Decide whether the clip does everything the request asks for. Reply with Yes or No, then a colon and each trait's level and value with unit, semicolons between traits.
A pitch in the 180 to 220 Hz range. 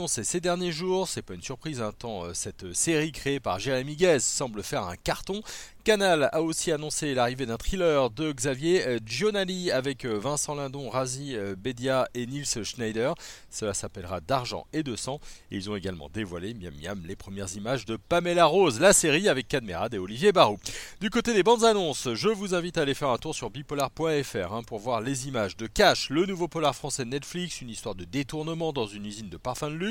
No: low, 135 Hz